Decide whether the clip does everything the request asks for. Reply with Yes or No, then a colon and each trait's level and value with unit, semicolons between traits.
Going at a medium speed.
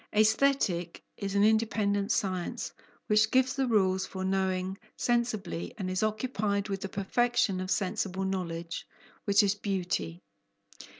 No: slow, 130 wpm